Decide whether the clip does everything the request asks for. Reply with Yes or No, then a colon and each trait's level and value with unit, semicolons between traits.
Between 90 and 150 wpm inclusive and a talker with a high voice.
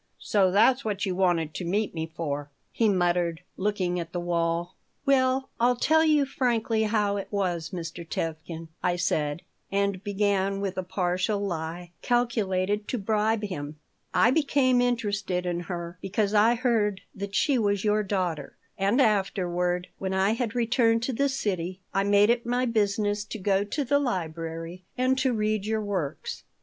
No: average, 165 wpm; high, 200 Hz